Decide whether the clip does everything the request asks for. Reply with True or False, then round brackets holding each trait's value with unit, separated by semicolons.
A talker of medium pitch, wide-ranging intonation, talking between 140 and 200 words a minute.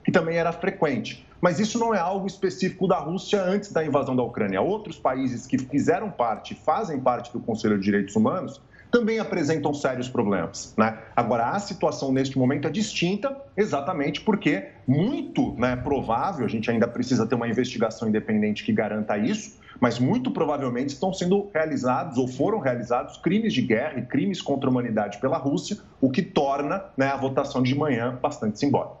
True (145 Hz; 7.3 semitones; 180 wpm)